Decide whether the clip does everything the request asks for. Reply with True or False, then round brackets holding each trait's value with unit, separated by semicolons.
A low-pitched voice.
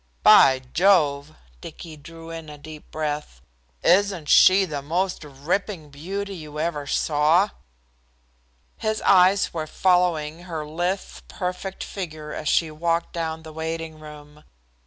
False (160 Hz)